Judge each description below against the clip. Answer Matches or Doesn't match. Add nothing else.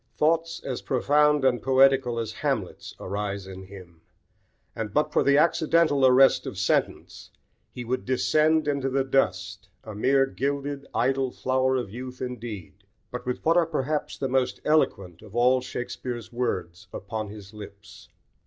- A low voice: Matches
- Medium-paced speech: Matches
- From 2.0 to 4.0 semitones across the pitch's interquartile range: Doesn't match